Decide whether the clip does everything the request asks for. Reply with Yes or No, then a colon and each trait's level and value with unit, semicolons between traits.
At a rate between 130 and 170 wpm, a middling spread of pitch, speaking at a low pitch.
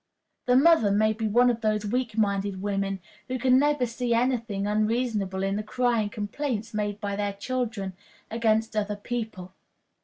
No: average, 165 wpm; average, 3.1 semitones; high, 215 Hz